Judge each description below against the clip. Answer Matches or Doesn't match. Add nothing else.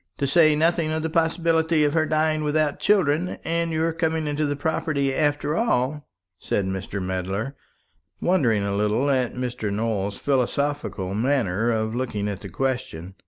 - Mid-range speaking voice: Matches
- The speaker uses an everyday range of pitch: Doesn't match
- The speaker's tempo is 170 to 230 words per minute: Doesn't match